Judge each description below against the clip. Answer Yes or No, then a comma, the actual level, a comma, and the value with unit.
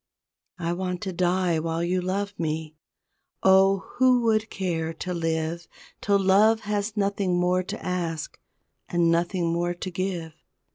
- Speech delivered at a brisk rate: No, average, 145 wpm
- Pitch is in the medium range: Yes, medium, 180 Hz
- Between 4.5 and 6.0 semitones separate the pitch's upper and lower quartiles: No, narrow, 2.5 semitones